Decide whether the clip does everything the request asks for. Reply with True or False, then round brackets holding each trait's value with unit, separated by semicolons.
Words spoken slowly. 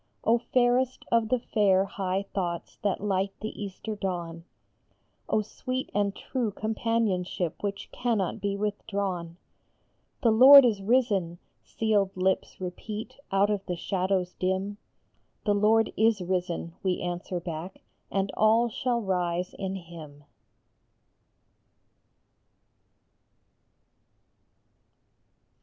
True (115 wpm)